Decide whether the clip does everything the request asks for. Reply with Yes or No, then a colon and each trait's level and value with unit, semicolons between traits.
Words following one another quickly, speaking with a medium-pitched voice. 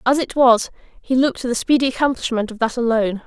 No: fast, 220 wpm; high, 245 Hz